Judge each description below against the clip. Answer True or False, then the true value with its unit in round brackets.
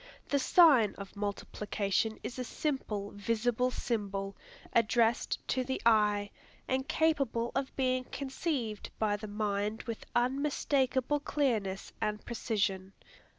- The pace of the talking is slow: True (115 wpm)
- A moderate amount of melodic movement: True (4.2 semitones)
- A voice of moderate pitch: False (230 Hz)